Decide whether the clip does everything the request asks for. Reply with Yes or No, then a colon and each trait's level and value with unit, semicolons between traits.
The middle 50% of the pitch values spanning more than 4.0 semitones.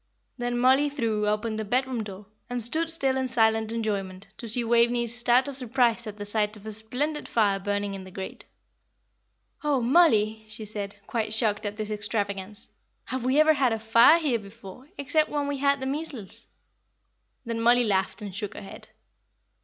No: average, 3.7 semitones